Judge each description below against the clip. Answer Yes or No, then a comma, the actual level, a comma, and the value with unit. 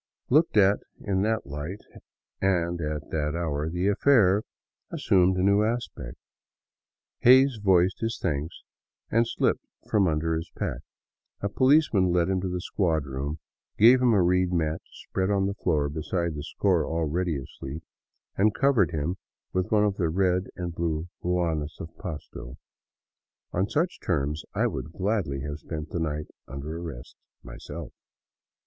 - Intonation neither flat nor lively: Yes, average, 4.3 semitones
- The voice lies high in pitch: No, very low, 90 Hz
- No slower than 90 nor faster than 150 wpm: No, average, 160 wpm